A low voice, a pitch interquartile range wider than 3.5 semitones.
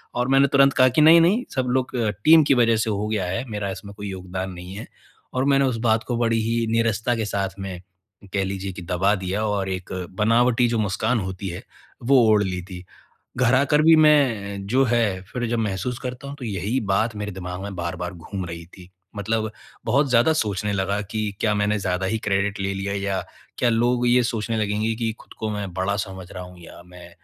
Yes: low, 105 Hz; average, 4.1 semitones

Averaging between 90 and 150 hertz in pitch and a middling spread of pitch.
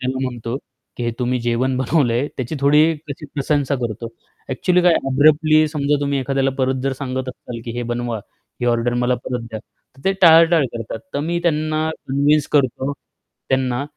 Yes: low, 135 Hz; average, 3.4 semitones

